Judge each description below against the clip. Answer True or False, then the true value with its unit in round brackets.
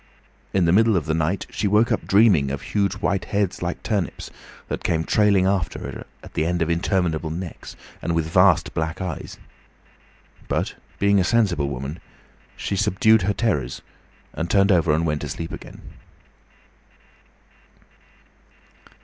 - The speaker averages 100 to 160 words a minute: True (155 wpm)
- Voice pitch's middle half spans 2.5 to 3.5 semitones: False (3.9 semitones)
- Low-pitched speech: True (90 Hz)